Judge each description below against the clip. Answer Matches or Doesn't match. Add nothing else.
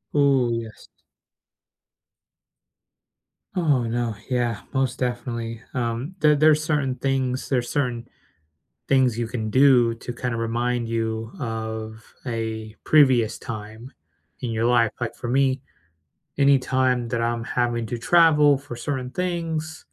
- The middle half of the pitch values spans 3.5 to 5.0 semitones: Doesn't match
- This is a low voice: Matches